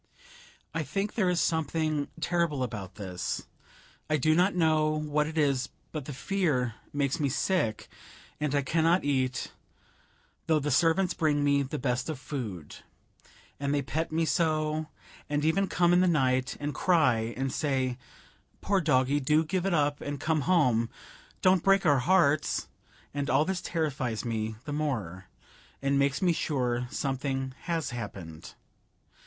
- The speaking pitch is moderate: Yes, medium, 145 Hz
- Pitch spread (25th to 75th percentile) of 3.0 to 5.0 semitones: Yes, average, 3.8 semitones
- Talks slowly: No, average, 155 wpm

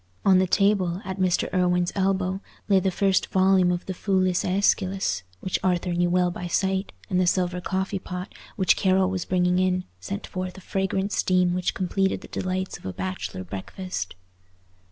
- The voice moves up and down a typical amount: No, narrow, 1.2 semitones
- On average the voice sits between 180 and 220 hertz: Yes, medium, 185 Hz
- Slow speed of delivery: No, average, 175 wpm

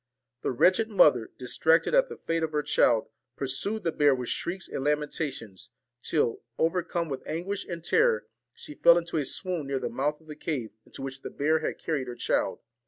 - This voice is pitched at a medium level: Yes, medium, 155 Hz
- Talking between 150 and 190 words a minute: No, average, 200 wpm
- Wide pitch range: No, average, 4.1 semitones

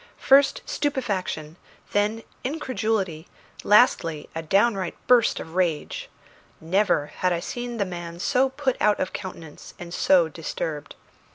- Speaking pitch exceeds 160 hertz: Yes, high, 190 Hz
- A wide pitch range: Yes, wide, 6.2 semitones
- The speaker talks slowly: Yes, slow, 125 wpm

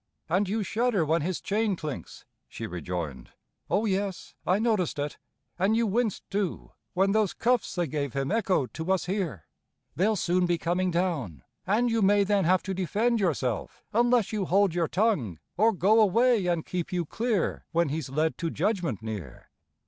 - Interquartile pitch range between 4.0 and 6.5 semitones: Yes, average, 4.7 semitones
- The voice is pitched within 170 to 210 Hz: Yes, medium, 185 Hz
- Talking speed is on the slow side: No, average, 180 wpm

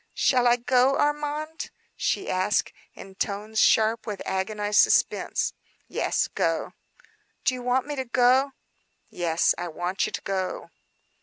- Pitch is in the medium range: No, high, 230 Hz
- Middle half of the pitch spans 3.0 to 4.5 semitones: No, average, 5.1 semitones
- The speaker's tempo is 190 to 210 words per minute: No, average, 140 wpm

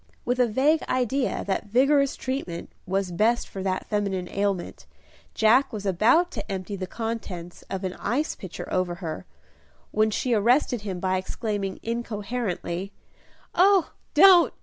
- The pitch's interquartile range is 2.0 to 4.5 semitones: No, average, 4.9 semitones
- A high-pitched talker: Yes, high, 210 Hz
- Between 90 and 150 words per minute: Yes, average, 145 wpm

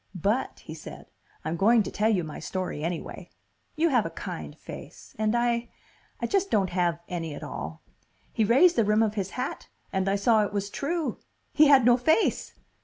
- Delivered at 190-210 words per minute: Yes, average, 195 wpm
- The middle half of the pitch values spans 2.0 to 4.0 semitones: No, average, 4.8 semitones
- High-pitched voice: Yes, high, 215 Hz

